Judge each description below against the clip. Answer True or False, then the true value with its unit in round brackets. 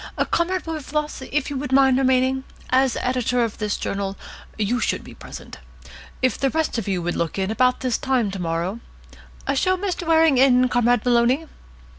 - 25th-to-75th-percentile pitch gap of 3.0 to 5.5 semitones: True (3.6 semitones)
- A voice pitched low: False (255 Hz)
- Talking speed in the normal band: True (170 wpm)